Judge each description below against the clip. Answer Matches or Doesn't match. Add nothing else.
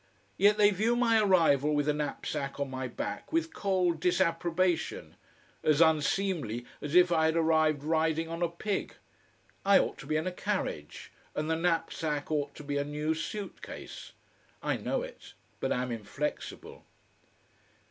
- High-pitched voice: Doesn't match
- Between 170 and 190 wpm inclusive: Doesn't match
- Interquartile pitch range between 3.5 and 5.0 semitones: Matches